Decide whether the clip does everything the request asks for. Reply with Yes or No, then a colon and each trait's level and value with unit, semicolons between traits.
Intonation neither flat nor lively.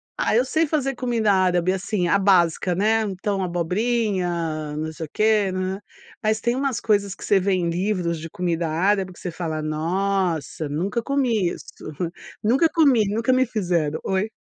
Yes: average, 4.3 semitones